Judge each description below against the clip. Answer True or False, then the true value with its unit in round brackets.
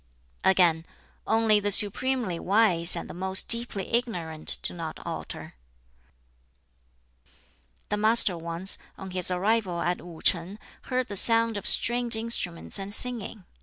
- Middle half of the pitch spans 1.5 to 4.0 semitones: False (4.4 semitones)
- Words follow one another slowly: True (130 wpm)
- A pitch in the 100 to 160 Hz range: False (195 Hz)